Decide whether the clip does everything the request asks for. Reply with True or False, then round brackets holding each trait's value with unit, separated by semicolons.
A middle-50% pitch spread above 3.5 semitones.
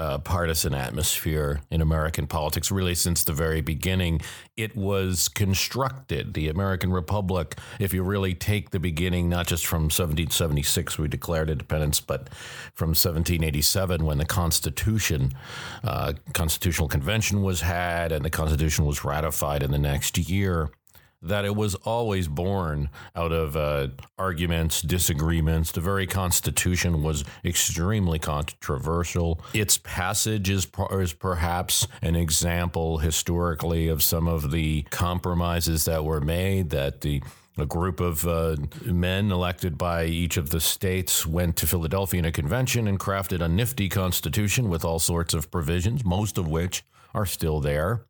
False (3.1 semitones)